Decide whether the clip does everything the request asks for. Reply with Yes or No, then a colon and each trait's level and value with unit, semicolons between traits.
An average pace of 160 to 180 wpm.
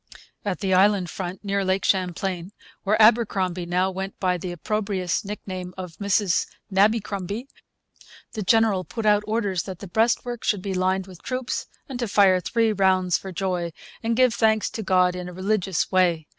Yes: average, 170 wpm